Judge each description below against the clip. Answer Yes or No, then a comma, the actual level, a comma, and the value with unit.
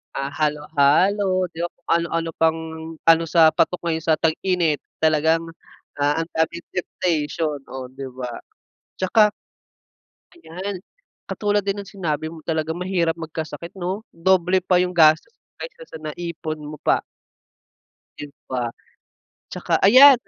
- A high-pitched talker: No, medium, 165 Hz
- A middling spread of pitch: Yes, average, 3.0 semitones